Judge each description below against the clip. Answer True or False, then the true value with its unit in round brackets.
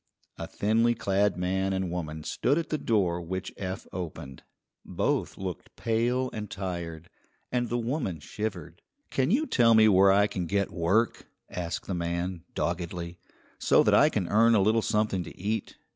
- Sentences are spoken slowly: False (170 wpm)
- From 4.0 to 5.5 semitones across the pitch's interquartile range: True (4.3 semitones)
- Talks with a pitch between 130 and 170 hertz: False (95 Hz)